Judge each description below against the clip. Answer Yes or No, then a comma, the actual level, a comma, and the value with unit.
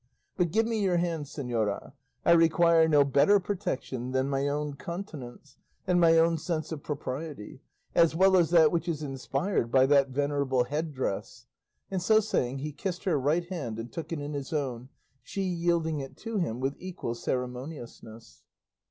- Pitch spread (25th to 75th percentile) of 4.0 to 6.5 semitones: Yes, average, 4.3 semitones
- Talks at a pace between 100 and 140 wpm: No, average, 175 wpm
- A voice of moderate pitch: Yes, medium, 150 Hz